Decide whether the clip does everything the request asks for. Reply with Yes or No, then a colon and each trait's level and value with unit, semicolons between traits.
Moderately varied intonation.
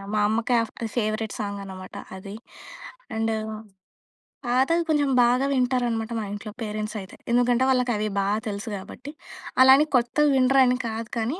Yes: average, 3.0 semitones